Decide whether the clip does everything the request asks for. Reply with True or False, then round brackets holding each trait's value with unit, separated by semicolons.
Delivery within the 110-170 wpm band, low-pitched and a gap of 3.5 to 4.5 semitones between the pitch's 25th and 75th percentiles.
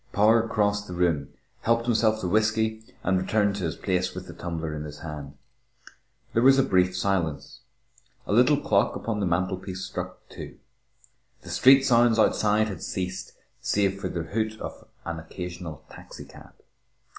True (160 wpm; 95 Hz; 3.9 semitones)